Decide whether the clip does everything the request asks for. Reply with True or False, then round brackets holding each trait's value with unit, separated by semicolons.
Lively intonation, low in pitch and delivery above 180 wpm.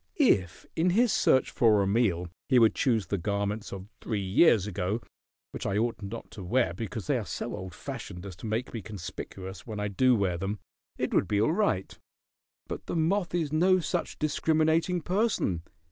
True (8.4 semitones; 110 Hz; 190 wpm)